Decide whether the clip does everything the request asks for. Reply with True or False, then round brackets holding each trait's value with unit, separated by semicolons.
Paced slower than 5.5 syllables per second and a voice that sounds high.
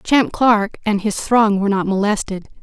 True (4.8 syllables/s; 210 Hz)